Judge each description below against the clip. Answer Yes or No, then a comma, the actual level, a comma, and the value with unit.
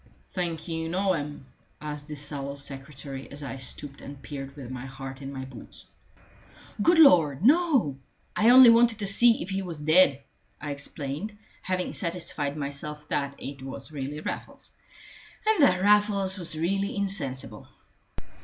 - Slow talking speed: No, average, 155 wpm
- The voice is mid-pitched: Yes, medium, 150 Hz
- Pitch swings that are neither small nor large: No, wide, 5.7 semitones